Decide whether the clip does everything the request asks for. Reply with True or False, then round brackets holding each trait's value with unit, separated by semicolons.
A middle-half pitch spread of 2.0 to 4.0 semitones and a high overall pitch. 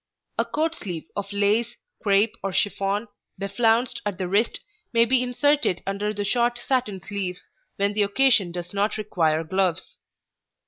True (3.2 semitones; 205 Hz)